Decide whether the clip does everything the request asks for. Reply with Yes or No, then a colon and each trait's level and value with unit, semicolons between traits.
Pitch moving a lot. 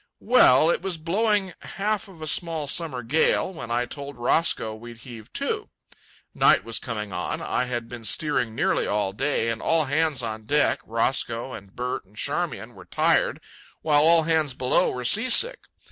Yes: wide, 6.0 semitones